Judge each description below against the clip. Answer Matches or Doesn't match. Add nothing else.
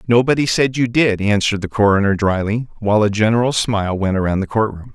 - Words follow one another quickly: Doesn't match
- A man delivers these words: Matches